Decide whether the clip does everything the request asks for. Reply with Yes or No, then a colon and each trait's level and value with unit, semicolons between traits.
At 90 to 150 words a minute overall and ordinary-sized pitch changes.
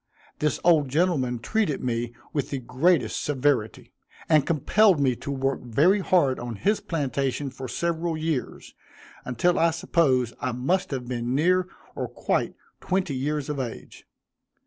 Yes: average, 145 wpm; average, 4.8 semitones